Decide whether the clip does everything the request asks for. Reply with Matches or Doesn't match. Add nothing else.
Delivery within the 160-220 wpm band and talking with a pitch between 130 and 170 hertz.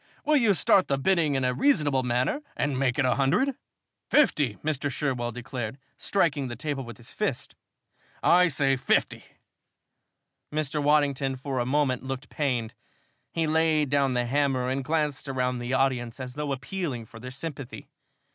Matches